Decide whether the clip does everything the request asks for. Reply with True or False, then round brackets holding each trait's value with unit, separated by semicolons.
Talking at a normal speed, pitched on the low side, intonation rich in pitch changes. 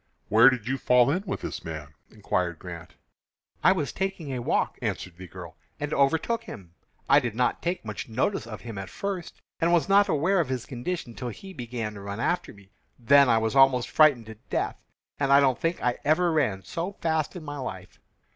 False (210 wpm; 130 Hz; 6.7 semitones)